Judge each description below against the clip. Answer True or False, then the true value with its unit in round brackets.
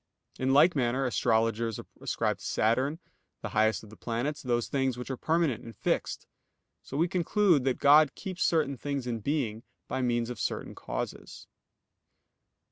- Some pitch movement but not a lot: True (4.1 semitones)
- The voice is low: True (130 Hz)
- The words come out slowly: False (160 wpm)